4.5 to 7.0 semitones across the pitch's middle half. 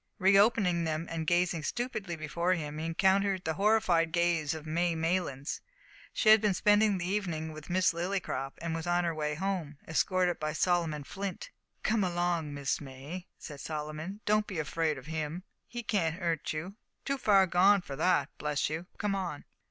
No: average, 3.6 semitones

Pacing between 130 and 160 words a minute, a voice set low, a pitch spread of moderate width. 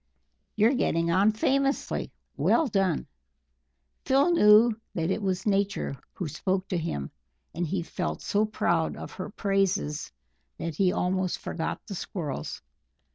No: slow, 135 wpm; high, 190 Hz; average, 3.7 semitones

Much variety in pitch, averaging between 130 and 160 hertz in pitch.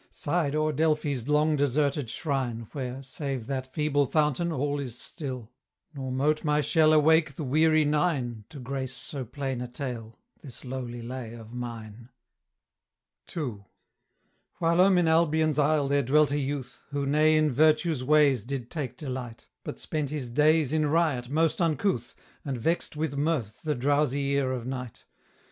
No: average, 3.3 semitones; medium, 140 Hz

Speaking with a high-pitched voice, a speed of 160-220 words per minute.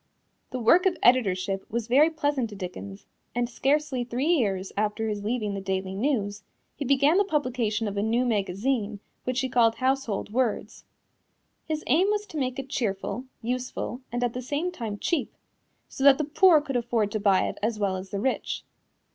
Yes: high, 245 Hz; average, 190 wpm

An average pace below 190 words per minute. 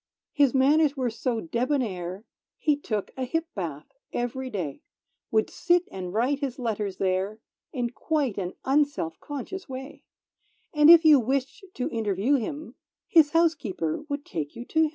Yes: average, 155 wpm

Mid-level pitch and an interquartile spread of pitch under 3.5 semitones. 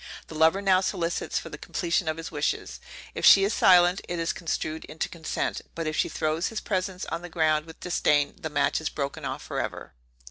Yes: medium, 165 Hz; narrow, 2.6 semitones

